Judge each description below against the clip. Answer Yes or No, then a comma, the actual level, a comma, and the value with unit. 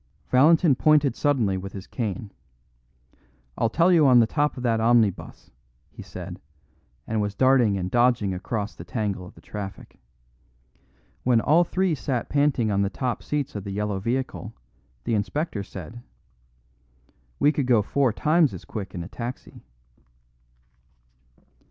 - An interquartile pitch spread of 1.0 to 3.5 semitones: No, wide, 5.6 semitones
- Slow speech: No, average, 150 wpm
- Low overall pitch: Yes, low, 120 Hz